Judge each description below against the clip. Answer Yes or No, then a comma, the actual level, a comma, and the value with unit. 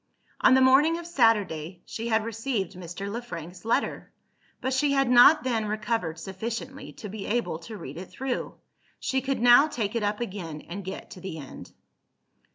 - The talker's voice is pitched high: Yes, high, 220 Hz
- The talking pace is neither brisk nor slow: Yes, average, 180 wpm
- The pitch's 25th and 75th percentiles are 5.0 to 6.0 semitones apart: Yes, average, 5.3 semitones